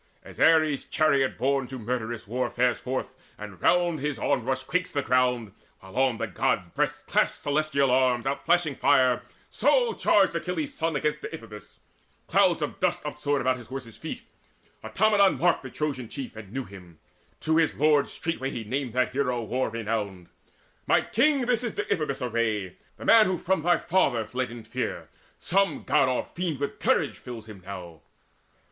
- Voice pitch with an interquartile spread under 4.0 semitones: No, average, 5.1 semitones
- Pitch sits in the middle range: No, low, 130 Hz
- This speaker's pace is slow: No, average, 170 wpm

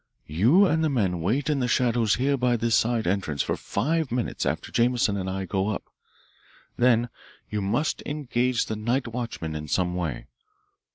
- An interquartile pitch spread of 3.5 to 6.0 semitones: Yes, average, 4.6 semitones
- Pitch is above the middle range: No, low, 115 Hz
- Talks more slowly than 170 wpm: No, average, 175 wpm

